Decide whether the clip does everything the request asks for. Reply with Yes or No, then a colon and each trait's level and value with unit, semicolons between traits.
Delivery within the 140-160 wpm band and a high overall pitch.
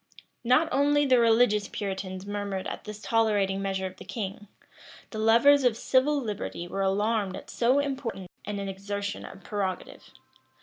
Yes: average, 150 wpm; high, 210 Hz